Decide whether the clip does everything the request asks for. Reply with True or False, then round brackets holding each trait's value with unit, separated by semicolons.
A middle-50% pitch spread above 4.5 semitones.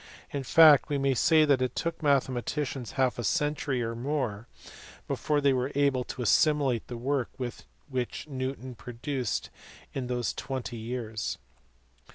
False (2.7 semitones)